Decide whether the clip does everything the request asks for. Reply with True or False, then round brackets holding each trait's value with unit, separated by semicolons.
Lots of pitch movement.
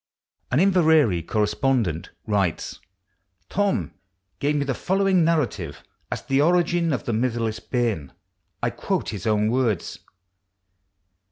True (7.5 semitones)